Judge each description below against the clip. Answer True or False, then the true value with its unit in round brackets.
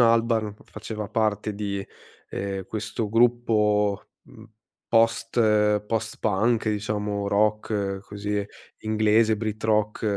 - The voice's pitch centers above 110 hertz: False (105 Hz)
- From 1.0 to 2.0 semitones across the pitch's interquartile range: True (1.4 semitones)